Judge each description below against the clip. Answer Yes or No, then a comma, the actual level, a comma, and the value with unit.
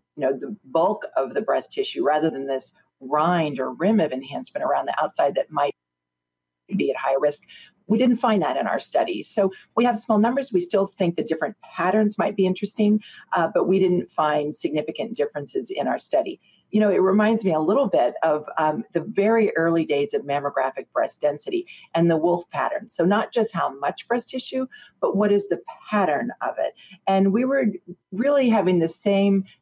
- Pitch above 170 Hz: Yes, high, 190 Hz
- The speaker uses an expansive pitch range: Yes, wide, 5.8 semitones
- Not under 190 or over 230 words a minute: Yes, average, 200 wpm